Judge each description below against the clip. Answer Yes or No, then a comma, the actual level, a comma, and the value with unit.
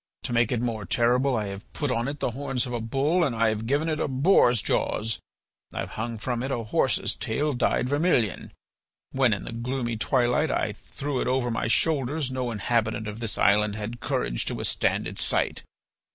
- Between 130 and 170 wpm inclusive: No, fast, 205 wpm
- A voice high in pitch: No, low, 120 Hz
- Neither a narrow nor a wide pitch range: Yes, average, 3.2 semitones